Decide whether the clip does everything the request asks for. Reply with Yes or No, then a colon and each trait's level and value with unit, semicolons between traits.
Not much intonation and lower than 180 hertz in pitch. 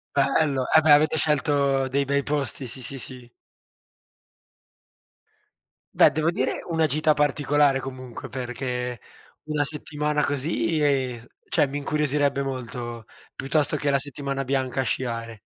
Yes: narrow, 2.3 semitones; medium, 140 Hz